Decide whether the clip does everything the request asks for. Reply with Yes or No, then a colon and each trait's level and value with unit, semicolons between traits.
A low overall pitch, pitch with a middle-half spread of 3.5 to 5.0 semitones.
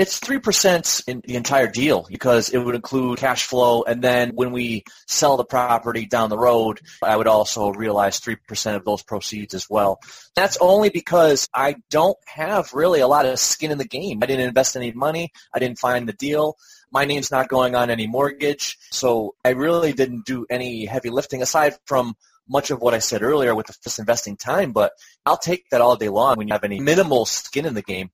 Yes: low, 125 Hz; average, 3.9 semitones